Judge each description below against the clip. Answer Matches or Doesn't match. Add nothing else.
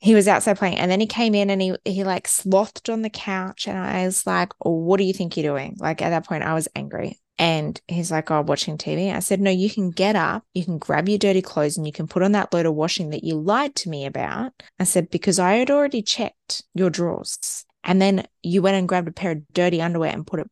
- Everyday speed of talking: Doesn't match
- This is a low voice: Doesn't match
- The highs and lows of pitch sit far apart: Doesn't match